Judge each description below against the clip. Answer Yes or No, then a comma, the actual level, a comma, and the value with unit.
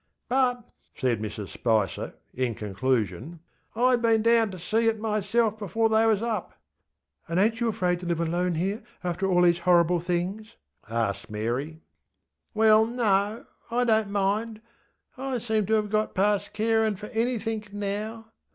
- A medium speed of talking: Yes, average, 155 wpm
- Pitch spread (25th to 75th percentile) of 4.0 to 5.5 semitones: Yes, average, 4.6 semitones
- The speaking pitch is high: Yes, high, 205 Hz